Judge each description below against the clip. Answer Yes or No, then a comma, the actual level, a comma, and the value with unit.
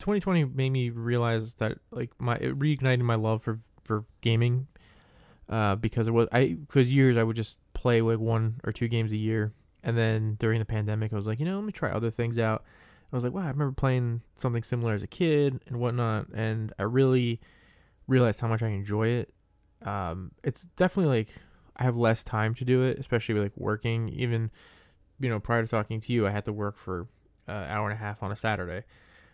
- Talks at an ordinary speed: No, fast, 220 wpm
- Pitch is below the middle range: Yes, low, 115 Hz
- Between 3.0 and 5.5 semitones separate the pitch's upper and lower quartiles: No, narrow, 2.6 semitones